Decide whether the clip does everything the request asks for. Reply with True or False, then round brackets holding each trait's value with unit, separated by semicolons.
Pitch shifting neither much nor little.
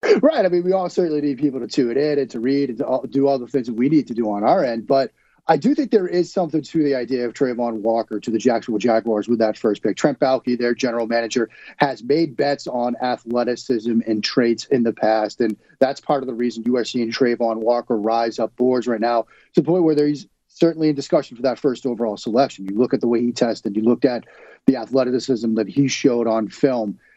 True (3.3 semitones)